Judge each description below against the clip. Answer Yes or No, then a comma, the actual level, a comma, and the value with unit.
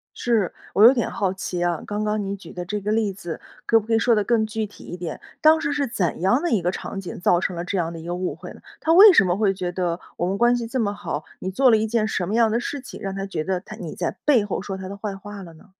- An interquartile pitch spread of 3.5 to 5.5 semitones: Yes, average, 3.8 semitones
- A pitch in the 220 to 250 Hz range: No, high, 200 Hz